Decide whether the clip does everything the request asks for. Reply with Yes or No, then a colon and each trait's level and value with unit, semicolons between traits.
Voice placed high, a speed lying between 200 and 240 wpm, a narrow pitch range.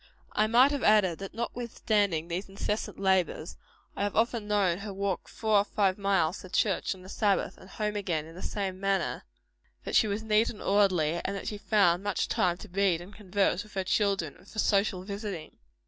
Yes: high, 200 Hz; fast, 205 wpm; narrow, 2.3 semitones